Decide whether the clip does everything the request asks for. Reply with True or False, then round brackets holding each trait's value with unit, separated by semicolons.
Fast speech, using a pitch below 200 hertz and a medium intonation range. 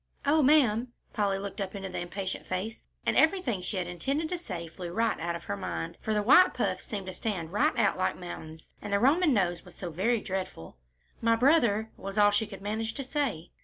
False (220 wpm; 205 Hz; 4.5 semitones)